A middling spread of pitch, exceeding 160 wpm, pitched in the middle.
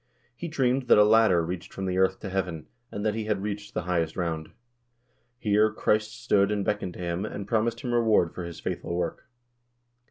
No: average, 3.4 semitones; average, 200 wpm; low, 100 Hz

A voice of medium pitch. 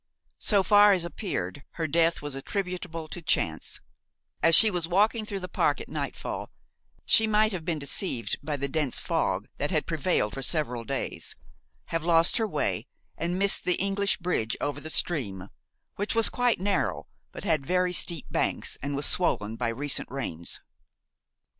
Yes: medium, 170 Hz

